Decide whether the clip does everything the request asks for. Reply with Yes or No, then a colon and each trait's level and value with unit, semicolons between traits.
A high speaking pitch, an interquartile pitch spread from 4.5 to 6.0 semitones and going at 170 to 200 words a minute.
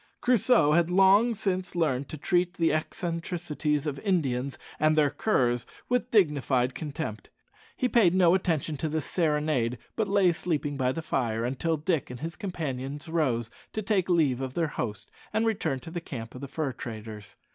No: medium, 155 Hz; average, 5.1 semitones; average, 175 wpm